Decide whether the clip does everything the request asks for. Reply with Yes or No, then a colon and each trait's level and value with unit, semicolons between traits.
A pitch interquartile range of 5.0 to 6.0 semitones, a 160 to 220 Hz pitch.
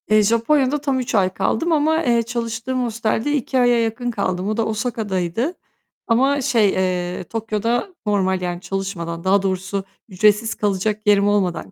No: average, 4.1 semitones; high, 215 Hz